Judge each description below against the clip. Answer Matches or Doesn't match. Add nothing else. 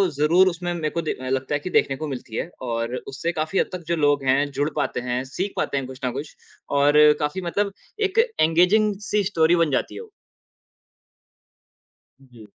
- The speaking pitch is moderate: Matches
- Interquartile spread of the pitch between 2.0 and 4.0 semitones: Doesn't match